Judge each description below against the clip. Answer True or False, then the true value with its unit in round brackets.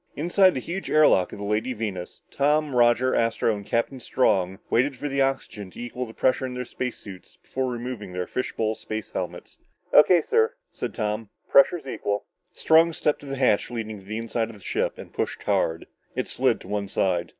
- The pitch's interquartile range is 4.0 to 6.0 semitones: True (4.6 semitones)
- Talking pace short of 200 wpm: False (205 wpm)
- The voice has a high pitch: False (120 Hz)